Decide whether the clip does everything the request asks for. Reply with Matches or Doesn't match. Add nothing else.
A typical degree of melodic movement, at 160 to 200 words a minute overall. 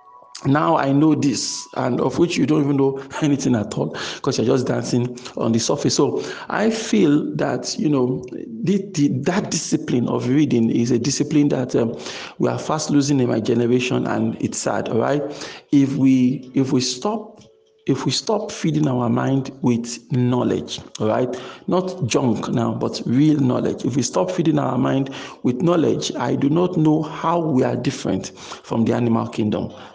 Matches